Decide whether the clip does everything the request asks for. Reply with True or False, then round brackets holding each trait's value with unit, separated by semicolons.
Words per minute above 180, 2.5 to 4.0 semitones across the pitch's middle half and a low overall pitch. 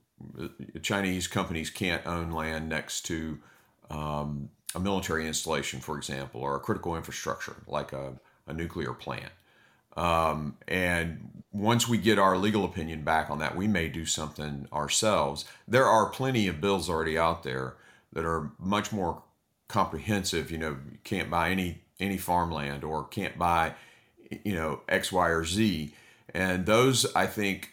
False (155 wpm; 3.6 semitones; 80 Hz)